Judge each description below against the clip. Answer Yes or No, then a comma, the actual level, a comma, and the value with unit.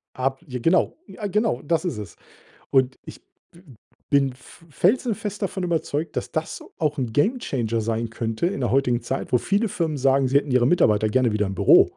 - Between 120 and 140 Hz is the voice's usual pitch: Yes, low, 135 Hz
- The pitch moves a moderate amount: No, wide, 6.1 semitones